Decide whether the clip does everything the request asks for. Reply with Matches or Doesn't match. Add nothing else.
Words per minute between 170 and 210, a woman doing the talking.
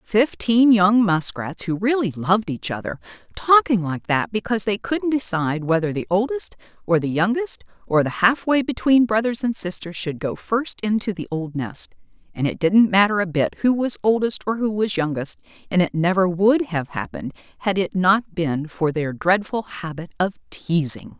Matches